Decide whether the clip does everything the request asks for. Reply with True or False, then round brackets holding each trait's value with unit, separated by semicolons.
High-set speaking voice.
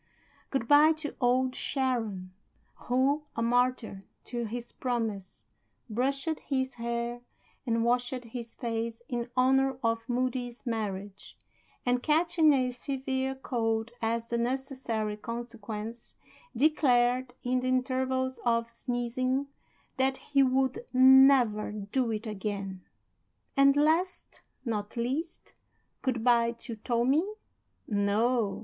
True (245 Hz)